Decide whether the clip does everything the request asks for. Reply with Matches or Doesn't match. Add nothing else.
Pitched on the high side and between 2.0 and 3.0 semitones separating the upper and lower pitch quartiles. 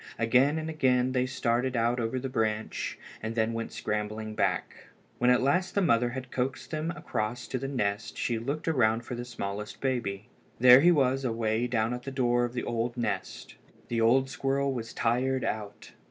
Doesn't match